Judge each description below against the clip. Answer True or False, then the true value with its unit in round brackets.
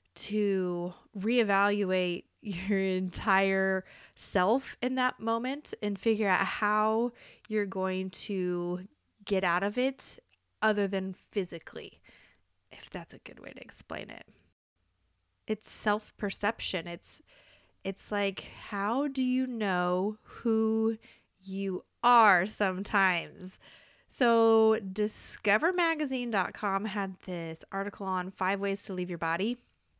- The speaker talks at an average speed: False (110 wpm)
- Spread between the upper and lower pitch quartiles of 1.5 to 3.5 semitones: True (2.8 semitones)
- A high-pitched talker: True (200 Hz)